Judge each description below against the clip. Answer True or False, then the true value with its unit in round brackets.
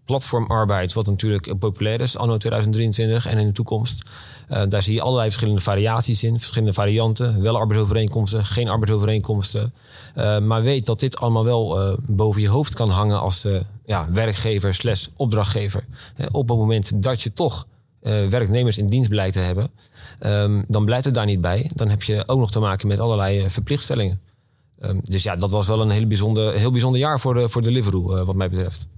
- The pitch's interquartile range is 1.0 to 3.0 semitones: True (2.5 semitones)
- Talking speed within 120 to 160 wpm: False (200 wpm)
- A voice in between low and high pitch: False (110 Hz)